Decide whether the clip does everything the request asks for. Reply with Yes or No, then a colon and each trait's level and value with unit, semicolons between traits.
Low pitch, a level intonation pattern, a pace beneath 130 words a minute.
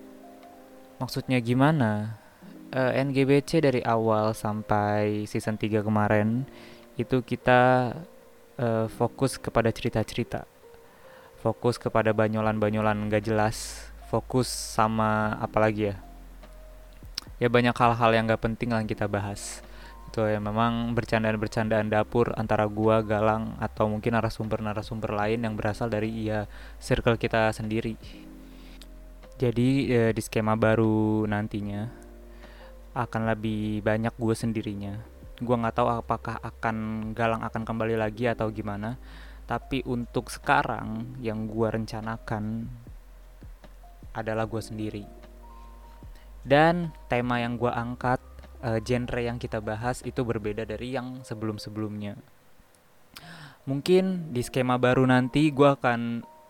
Yes: low, 115 Hz; narrow, 2.1 semitones; average, 115 wpm